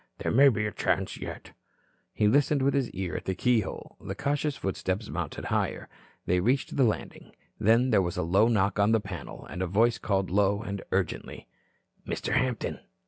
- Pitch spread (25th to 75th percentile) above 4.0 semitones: Yes, average, 4.4 semitones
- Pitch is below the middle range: Yes, low, 105 Hz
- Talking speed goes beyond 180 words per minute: Yes, average, 190 wpm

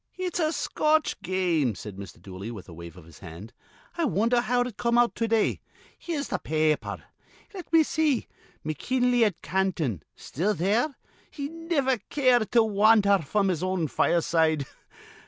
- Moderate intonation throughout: No, wide, 8.3 semitones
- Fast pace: No, average, 165 wpm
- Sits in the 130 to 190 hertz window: No, high, 205 Hz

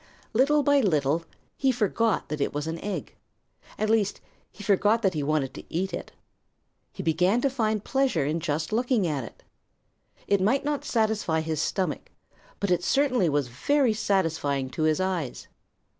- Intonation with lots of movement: Yes, wide, 6.4 semitones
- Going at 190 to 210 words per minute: No, average, 170 wpm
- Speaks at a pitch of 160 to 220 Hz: Yes, high, 190 Hz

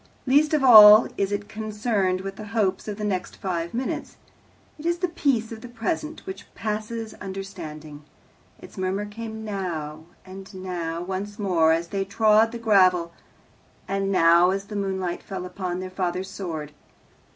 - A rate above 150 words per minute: Yes, average, 160 wpm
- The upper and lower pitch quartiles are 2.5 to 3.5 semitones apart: Yes, average, 3.2 semitones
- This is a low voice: No, high, 195 Hz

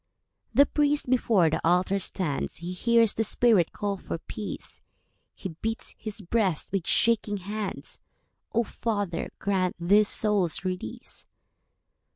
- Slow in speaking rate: Yes, slow, 130 wpm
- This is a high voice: Yes, high, 200 Hz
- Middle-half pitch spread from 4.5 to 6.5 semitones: No, average, 3.7 semitones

